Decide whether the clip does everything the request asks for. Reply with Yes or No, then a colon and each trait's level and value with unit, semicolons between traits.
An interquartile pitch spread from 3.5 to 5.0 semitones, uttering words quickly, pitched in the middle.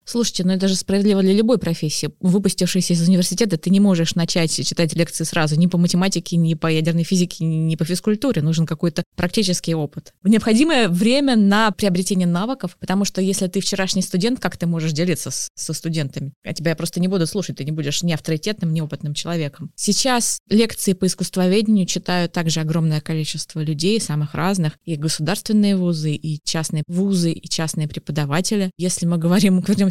No: average, 3.1 semitones; fast, 180 wpm; medium, 175 Hz